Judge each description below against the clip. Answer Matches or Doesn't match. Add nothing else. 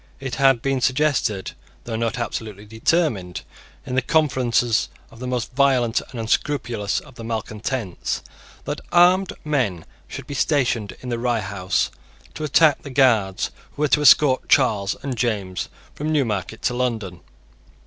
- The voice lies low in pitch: Matches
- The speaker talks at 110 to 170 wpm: Matches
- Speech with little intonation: Doesn't match